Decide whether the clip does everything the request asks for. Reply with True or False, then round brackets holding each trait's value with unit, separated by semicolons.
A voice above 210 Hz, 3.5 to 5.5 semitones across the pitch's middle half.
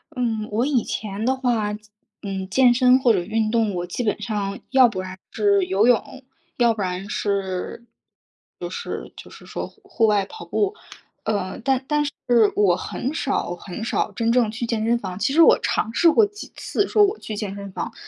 True (220 Hz; 4.1 semitones)